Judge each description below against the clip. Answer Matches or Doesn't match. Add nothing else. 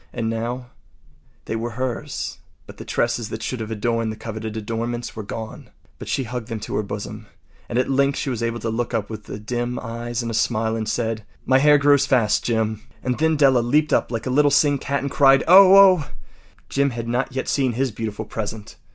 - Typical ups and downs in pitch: Matches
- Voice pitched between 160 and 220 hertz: Doesn't match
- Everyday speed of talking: Doesn't match